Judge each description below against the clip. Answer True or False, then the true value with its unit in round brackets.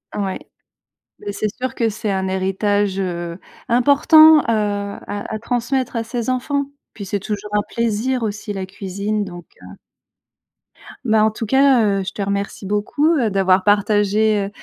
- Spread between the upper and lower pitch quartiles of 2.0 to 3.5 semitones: True (3.0 semitones)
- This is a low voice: False (210 Hz)